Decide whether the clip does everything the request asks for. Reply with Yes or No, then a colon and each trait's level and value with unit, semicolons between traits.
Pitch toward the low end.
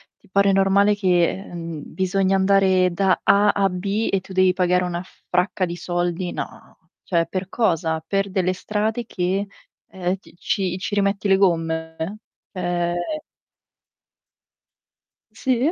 No: medium, 185 Hz